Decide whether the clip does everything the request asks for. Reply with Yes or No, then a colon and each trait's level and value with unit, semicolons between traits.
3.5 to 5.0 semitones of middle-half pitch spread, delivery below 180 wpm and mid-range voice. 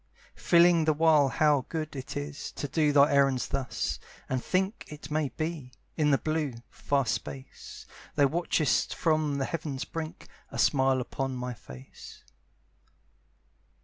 No: average, 2.8 semitones; average, 145 wpm; medium, 145 Hz